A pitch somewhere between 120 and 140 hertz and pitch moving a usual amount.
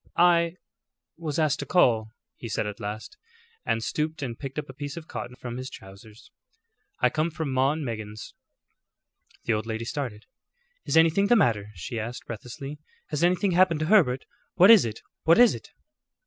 No: low, 135 Hz; wide, 6.5 semitones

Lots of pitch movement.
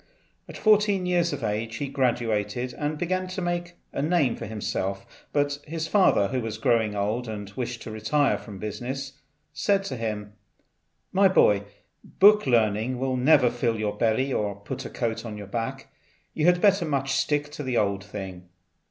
Yes: wide, 6.0 semitones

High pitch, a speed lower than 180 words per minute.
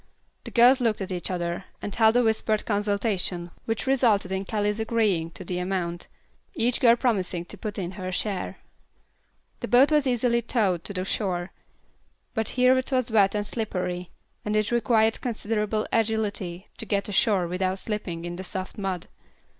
Yes: high, 205 Hz; average, 170 wpm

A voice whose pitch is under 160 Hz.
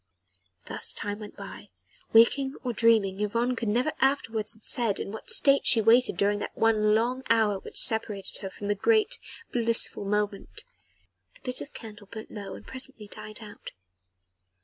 No: high, 220 Hz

